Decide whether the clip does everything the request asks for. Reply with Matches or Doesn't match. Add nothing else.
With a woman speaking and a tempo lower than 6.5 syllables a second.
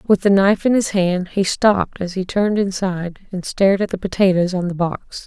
Matches